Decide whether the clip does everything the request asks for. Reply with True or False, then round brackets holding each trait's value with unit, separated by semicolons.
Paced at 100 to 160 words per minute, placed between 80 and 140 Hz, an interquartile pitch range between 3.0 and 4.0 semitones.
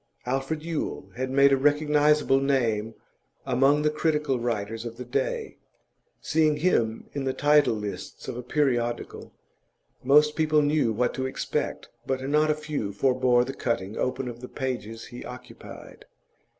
True (150 wpm; 135 Hz; 3.7 semitones)